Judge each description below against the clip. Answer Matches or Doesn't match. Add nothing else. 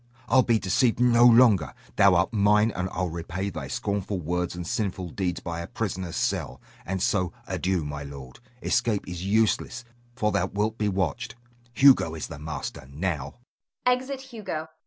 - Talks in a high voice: Doesn't match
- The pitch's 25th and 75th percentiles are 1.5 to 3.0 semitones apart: Doesn't match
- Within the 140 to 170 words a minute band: Matches